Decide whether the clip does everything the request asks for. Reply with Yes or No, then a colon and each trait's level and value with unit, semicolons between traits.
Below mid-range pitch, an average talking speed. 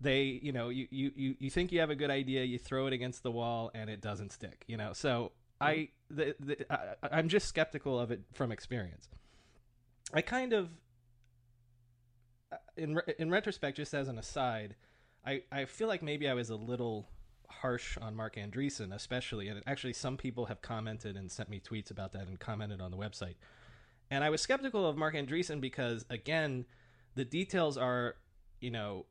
Yes: low, 125 Hz; average, 190 wpm